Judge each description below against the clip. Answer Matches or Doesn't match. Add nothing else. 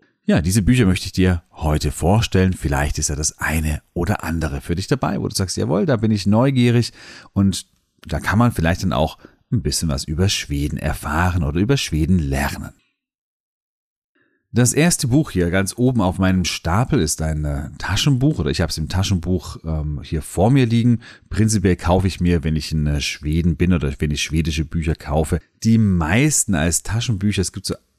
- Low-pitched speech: Matches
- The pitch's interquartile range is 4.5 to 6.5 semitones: Matches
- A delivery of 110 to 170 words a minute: Doesn't match